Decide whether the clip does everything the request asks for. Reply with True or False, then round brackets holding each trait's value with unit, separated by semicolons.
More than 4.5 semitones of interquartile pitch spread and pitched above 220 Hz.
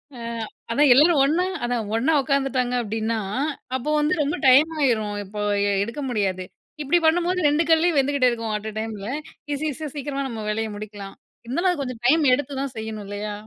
True (5.2 semitones; 255 Hz)